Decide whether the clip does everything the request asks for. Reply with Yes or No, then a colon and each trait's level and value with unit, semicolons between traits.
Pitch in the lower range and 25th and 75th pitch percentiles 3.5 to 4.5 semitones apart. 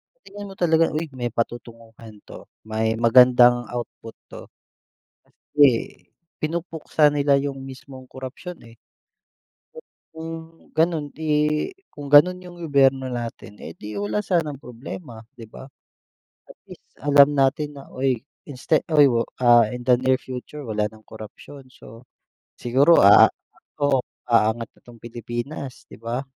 Yes: low, 130 Hz; average, 4.0 semitones